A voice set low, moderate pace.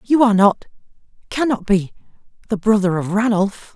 No: high, 210 Hz; average, 145 wpm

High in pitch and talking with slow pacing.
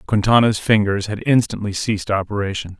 No: low, 105 Hz; slow, 130 wpm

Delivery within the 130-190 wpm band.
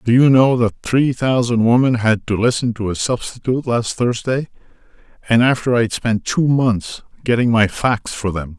Yes: average, 175 wpm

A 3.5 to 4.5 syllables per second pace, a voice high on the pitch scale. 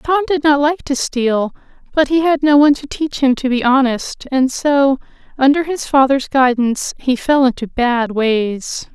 Yes: 4.4 syllables/s; very high, 270 Hz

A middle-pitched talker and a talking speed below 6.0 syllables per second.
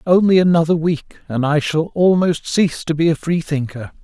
Yes: medium, 160 Hz; 5.1 syllables/s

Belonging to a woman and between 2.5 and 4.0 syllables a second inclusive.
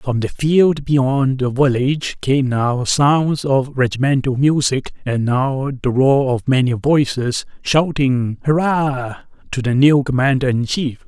No: male; 3.9 syllables/s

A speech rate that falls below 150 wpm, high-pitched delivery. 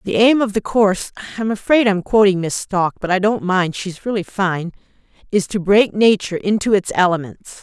No: average, 180 wpm; high, 200 Hz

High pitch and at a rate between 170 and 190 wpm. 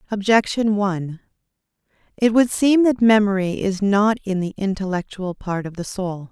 No: high, 200 Hz; average, 150 wpm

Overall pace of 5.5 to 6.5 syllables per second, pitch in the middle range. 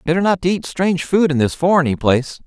Yes: 6.4 syllables/s; medium, 165 Hz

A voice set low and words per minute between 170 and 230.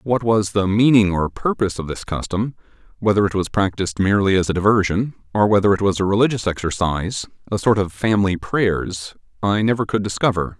Yes: low, 100 Hz; average, 185 wpm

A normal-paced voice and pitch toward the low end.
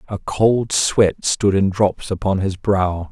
Yes: average, 175 wpm; low, 100 Hz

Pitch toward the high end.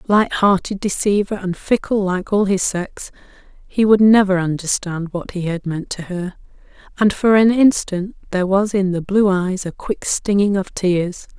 Yes: high, 195 Hz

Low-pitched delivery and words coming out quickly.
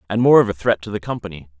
Yes: low, 100 Hz; fast, 300 wpm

